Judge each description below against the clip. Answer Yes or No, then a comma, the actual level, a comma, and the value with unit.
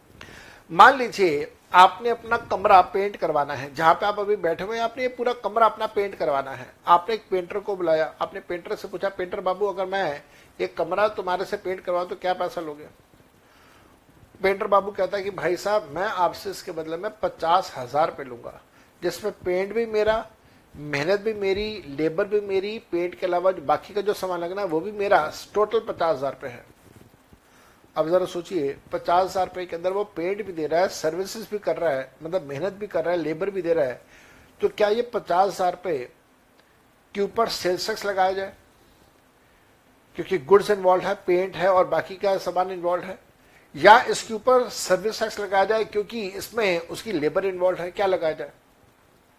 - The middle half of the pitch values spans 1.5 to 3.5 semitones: Yes, average, 3.0 semitones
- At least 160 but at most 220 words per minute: Yes, fast, 190 wpm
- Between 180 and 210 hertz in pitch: Yes, high, 190 Hz